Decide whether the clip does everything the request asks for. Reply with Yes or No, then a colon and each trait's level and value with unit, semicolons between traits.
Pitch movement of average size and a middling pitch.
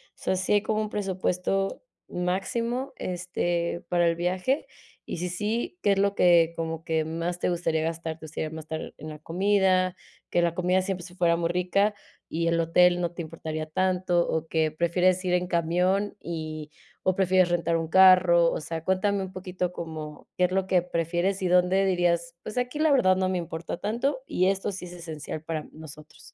No: narrow, 2.2 semitones; medium, 180 Hz